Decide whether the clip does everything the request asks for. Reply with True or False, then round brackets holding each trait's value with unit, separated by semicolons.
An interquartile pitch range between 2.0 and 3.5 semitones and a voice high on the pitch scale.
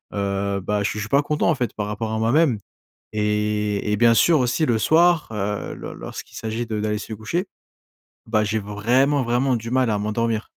False (3.2 semitones; 110 Hz)